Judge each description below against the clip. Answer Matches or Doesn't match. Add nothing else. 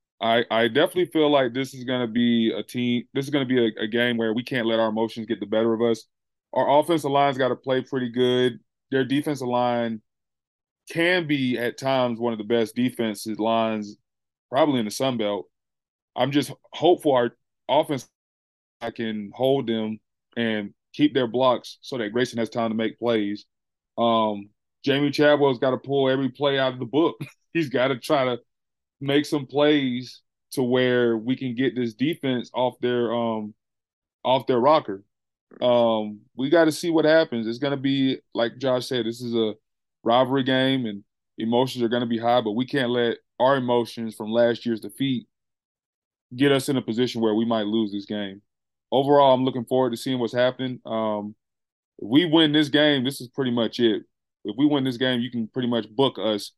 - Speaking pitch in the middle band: Doesn't match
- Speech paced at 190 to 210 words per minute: Matches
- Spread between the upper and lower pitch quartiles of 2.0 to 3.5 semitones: Matches